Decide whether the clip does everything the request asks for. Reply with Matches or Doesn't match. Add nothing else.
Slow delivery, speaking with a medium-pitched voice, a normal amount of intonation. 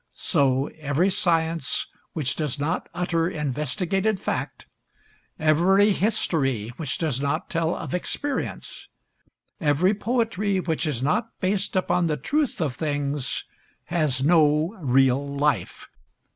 Matches